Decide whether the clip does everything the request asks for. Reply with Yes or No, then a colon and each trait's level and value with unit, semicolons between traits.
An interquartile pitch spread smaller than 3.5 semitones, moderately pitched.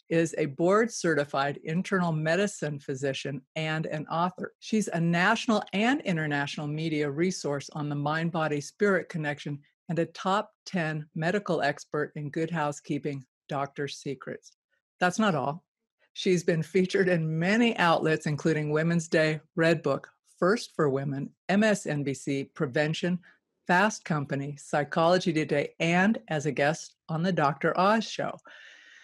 No: average, 3.8 semitones; medium, 160 Hz